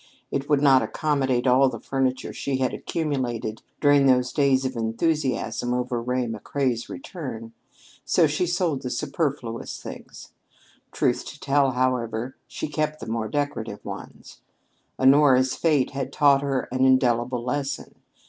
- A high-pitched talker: No, low, 130 Hz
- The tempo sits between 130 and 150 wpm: Yes, average, 145 wpm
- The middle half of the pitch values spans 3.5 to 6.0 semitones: No, narrow, 2.6 semitones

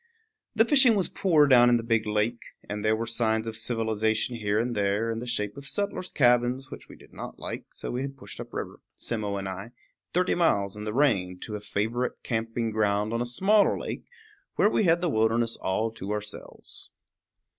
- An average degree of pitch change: Yes, average, 3.3 semitones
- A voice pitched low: Yes, low, 115 Hz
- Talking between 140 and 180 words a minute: No, fast, 205 wpm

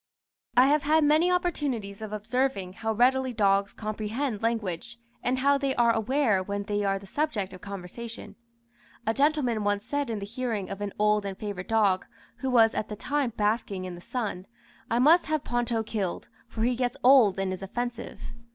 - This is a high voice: Yes, high, 225 Hz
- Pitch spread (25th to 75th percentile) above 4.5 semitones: No, average, 4.2 semitones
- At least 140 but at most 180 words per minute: No, average, 190 wpm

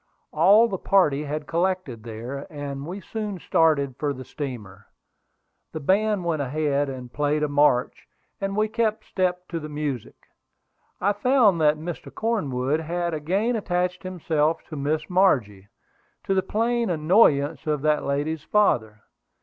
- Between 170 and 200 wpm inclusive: No, average, 150 wpm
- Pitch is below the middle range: No, medium, 155 Hz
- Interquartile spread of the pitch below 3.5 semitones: No, average, 5.1 semitones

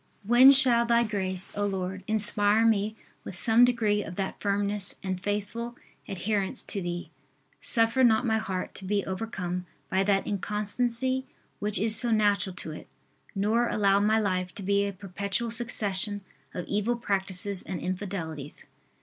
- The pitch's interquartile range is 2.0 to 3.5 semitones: Yes, average, 2.8 semitones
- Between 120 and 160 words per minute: Yes, average, 155 wpm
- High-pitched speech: Yes, high, 205 Hz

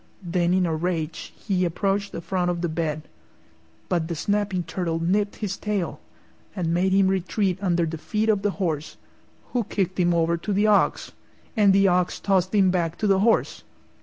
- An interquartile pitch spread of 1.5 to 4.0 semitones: Yes, average, 2.8 semitones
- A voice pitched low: No, medium, 185 Hz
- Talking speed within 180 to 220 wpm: Yes, average, 190 wpm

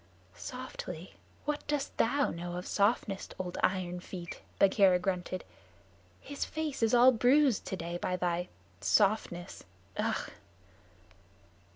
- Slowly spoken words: Yes, slow, 110 wpm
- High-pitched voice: Yes, high, 195 Hz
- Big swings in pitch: Yes, wide, 5.9 semitones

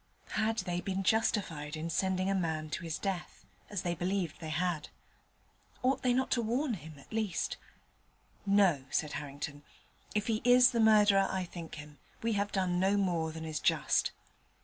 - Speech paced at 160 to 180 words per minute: Yes, average, 175 wpm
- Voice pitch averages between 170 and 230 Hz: Yes, medium, 185 Hz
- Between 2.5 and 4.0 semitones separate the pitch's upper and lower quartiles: No, average, 4.7 semitones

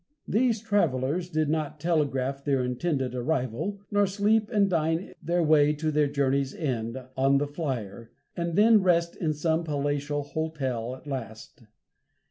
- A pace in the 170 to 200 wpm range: No, average, 145 wpm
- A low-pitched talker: No, medium, 150 Hz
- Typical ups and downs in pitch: Yes, average, 4.2 semitones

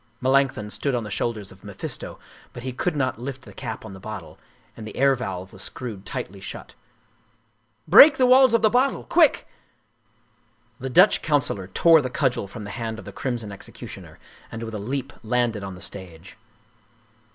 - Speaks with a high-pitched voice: No, low, 115 Hz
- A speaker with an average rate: Yes, average, 190 wpm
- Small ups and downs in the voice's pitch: No, average, 5.0 semitones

